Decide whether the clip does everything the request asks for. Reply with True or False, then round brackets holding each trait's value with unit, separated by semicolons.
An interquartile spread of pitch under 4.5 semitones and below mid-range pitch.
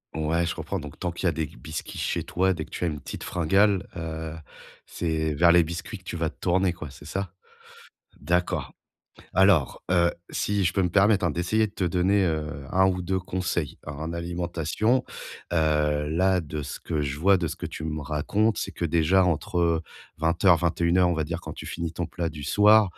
True (2.9 semitones; 85 Hz)